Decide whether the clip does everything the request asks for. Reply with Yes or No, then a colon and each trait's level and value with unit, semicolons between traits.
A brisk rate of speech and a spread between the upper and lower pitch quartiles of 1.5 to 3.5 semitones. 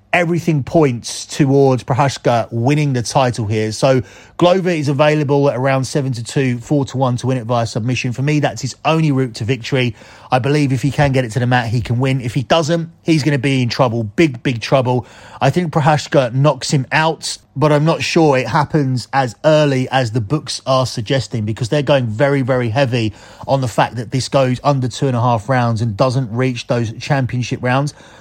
Yes: fast, 215 wpm; average, 2.9 semitones